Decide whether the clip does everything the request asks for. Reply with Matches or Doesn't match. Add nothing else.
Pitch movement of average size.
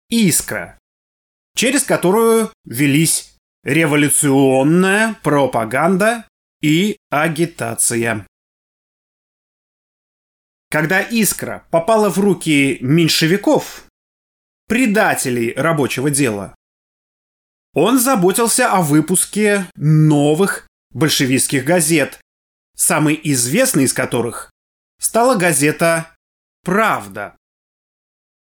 Doesn't match